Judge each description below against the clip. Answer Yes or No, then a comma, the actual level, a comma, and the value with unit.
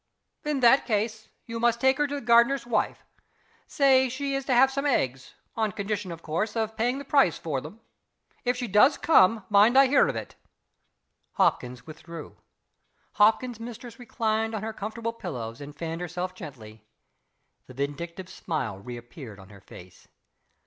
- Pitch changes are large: Yes, wide, 7.5 semitones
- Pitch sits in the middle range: No, high, 215 Hz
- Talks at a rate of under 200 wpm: Yes, average, 165 wpm